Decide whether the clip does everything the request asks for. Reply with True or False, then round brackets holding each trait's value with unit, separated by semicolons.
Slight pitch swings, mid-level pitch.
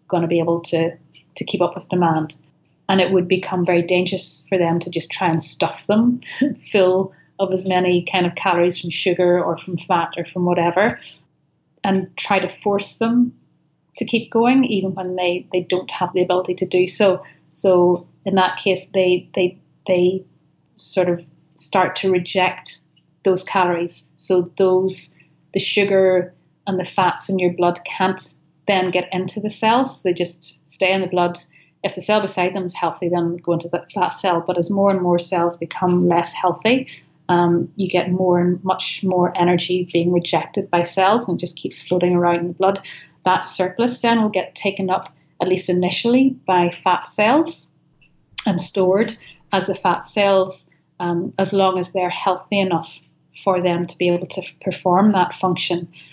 True (1.7 semitones; 180 Hz)